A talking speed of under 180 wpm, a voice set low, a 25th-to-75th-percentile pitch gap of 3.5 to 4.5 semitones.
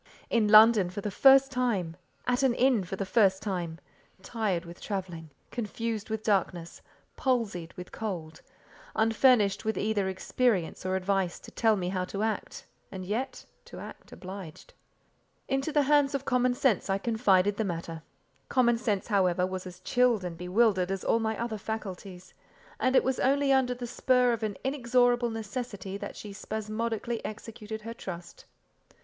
No: average, 160 wpm; high, 215 Hz; average, 4.2 semitones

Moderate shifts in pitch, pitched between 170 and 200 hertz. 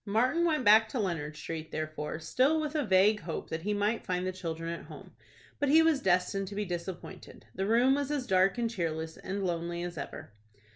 No: wide, 5.8 semitones; high, 190 Hz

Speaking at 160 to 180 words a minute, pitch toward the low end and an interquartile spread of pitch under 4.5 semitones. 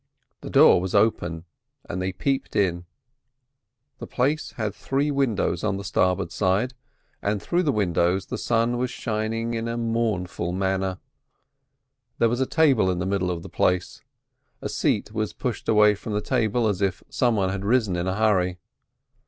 Yes: average, 175 wpm; low, 105 Hz; average, 3.9 semitones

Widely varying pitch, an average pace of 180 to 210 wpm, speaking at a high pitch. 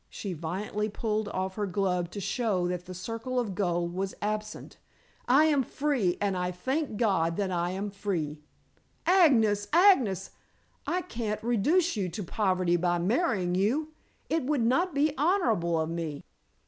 No: wide, 6.0 semitones; average, 160 wpm; high, 205 Hz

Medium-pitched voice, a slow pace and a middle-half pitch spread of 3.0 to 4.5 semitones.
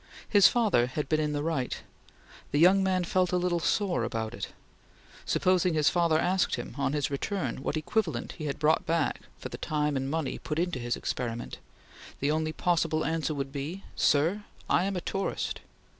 No: medium, 155 Hz; average, 190 wpm; average, 4.2 semitones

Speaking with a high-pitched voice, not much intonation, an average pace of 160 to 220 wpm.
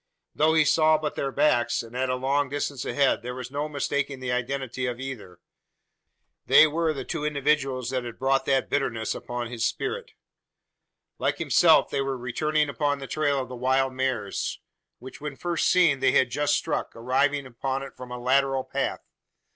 No: low, 135 Hz; narrow, 2.3 semitones; average, 185 wpm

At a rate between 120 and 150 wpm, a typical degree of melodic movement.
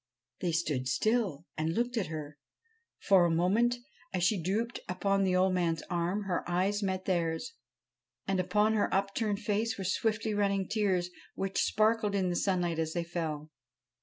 No: average, 165 wpm; average, 3.3 semitones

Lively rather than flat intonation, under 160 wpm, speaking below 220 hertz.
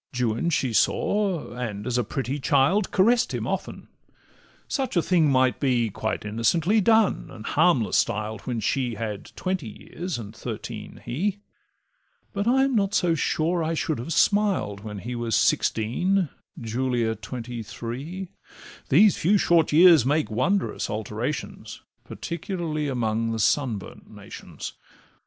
Yes: wide, 7.9 semitones; average, 140 wpm; low, 135 Hz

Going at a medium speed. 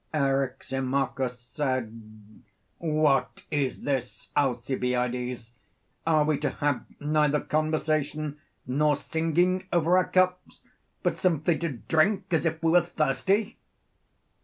No: slow, 110 wpm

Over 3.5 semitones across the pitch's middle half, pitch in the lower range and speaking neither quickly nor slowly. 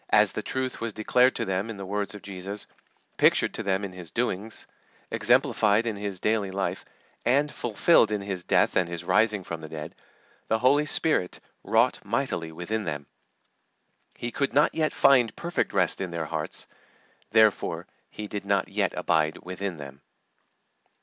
Yes: average, 4.0 semitones; low, 100 Hz; average, 170 wpm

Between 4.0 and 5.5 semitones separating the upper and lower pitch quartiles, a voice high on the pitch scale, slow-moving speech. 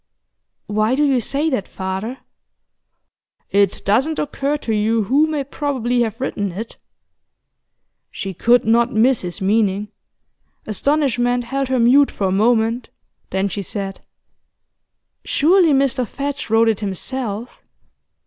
Yes: average, 4.5 semitones; high, 235 Hz; slow, 130 wpm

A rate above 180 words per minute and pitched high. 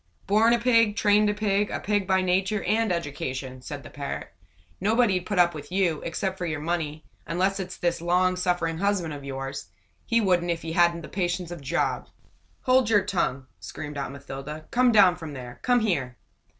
No: average, 190 wpm; medium, 175 Hz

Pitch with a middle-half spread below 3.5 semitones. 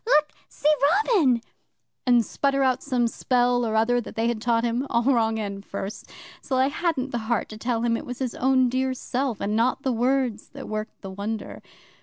Yes: average, 2.7 semitones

